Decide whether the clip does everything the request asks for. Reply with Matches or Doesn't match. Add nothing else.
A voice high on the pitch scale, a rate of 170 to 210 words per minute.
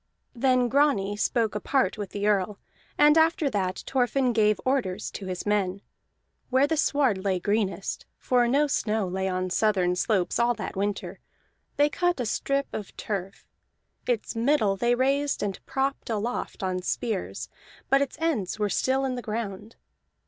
Doesn't match